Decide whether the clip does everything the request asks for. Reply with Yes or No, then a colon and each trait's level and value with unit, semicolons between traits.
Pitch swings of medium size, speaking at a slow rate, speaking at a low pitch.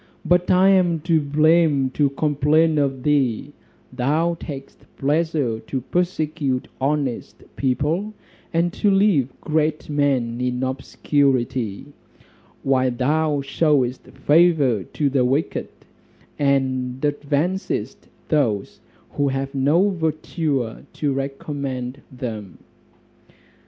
No: average, 3.3 semitones; slow, 100 wpm; medium, 145 Hz